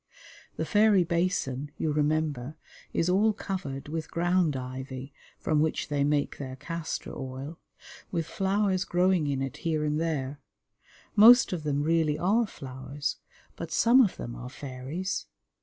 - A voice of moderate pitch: Yes, medium, 155 Hz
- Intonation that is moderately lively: Yes, average, 4.8 semitones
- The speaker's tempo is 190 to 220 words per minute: No, average, 145 wpm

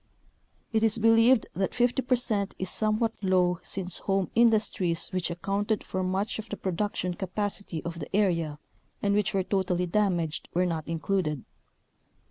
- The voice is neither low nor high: No, high, 195 Hz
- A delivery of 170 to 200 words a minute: No, average, 150 wpm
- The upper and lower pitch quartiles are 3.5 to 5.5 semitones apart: No, average, 3.1 semitones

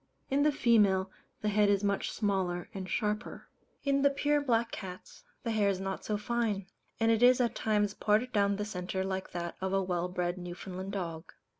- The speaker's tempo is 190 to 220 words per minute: Yes, average, 195 wpm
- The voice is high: Yes, high, 200 Hz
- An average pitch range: Yes, average, 3.2 semitones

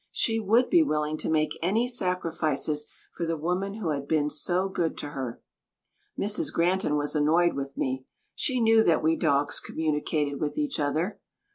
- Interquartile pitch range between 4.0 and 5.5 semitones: Yes, average, 4.7 semitones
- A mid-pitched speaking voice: Yes, medium, 160 Hz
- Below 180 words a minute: Yes, average, 170 wpm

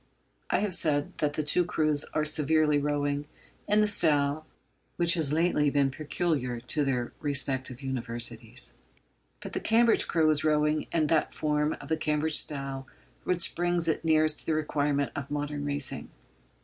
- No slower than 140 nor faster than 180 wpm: Yes, average, 160 wpm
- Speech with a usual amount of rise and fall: No, narrow, 2.0 semitones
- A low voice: No, medium, 150 Hz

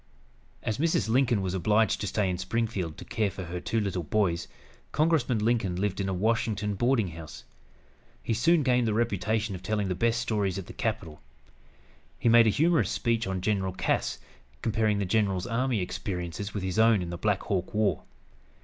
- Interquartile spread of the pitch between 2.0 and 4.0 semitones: Yes, average, 3.5 semitones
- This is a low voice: Yes, low, 105 Hz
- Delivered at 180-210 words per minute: Yes, average, 185 wpm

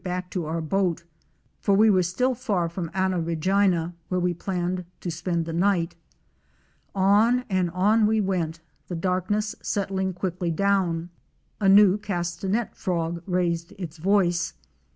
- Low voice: No, medium, 185 Hz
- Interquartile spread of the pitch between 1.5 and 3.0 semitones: Yes, narrow, 2.6 semitones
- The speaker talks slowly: No, average, 145 wpm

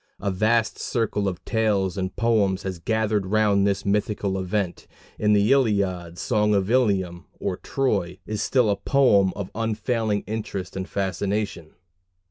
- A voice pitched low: Yes, low, 100 Hz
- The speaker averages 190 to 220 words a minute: No, average, 145 wpm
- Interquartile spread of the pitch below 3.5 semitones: Yes, narrow, 2.4 semitones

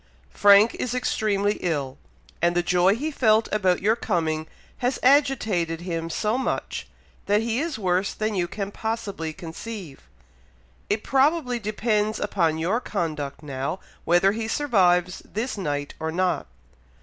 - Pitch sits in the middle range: No, high, 200 Hz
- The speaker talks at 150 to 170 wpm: No, average, 140 wpm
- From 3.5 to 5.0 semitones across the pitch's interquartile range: Yes, average, 4.6 semitones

